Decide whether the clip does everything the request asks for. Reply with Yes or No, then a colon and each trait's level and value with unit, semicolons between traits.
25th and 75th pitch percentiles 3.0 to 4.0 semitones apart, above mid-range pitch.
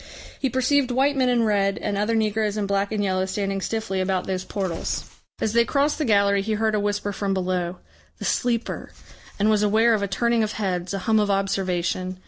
No: narrow, 2.4 semitones; high, 205 Hz